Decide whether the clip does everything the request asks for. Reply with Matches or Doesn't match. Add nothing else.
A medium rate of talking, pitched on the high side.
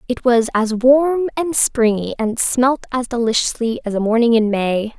Matches